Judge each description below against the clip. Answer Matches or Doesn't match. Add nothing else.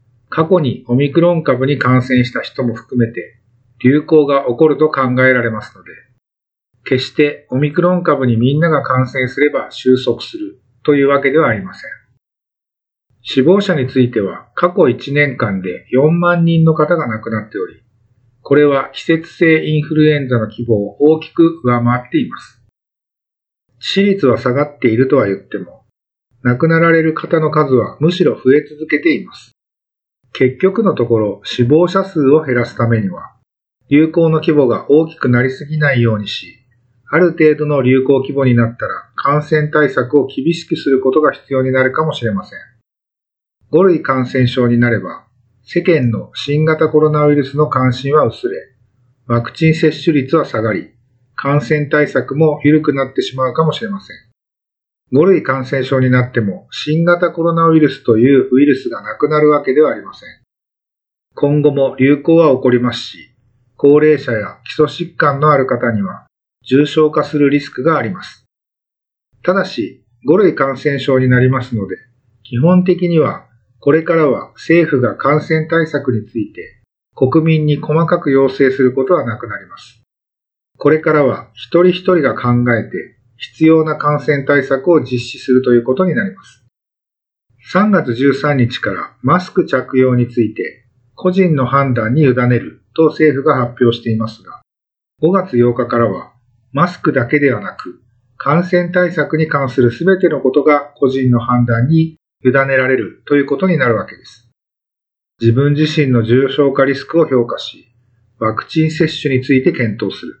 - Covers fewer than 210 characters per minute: Doesn't match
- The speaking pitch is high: Doesn't match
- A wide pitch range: Doesn't match